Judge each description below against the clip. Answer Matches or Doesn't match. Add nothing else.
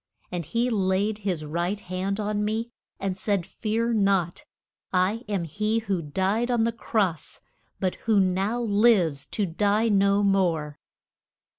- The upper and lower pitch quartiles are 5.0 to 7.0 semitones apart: Doesn't match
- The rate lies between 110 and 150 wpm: Matches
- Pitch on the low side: Doesn't match